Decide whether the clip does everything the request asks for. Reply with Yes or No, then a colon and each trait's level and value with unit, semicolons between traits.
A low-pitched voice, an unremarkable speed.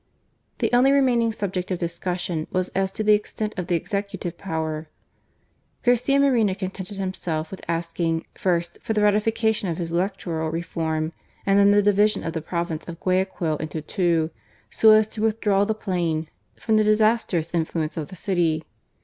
No: medium, 185 Hz; average, 165 wpm